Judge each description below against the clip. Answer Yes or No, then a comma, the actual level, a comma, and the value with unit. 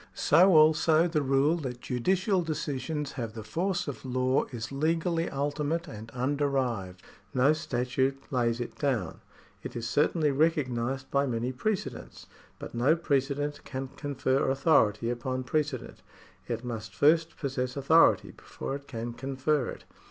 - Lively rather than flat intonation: No, average, 3.7 semitones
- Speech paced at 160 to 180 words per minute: No, average, 145 wpm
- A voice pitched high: No, low, 135 Hz